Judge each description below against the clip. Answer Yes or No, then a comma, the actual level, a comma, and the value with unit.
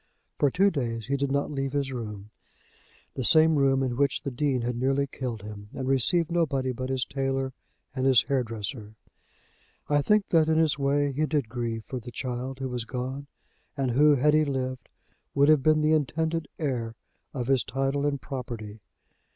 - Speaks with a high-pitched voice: No, low, 135 Hz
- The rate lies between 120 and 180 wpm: No, average, 190 wpm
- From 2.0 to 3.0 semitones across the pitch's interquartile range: Yes, average, 2.7 semitones